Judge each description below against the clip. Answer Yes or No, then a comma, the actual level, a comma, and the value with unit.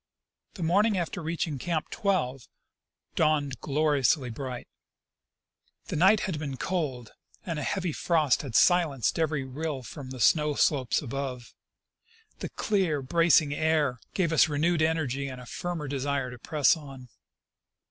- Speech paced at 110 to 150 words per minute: Yes, average, 140 wpm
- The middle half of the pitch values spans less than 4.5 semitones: Yes, average, 3.8 semitones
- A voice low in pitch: No, medium, 150 Hz